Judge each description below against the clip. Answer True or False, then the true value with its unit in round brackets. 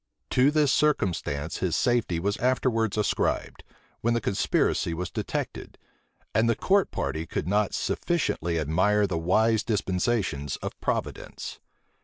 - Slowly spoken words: True (130 wpm)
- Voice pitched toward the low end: True (105 Hz)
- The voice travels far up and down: True (5.7 semitones)